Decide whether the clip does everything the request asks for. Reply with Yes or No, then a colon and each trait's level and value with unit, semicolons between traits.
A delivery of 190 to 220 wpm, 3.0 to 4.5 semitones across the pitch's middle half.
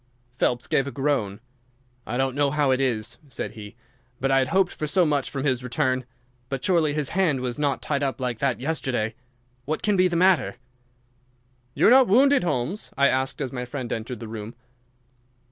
Yes: average, 195 wpm; average, 3.7 semitones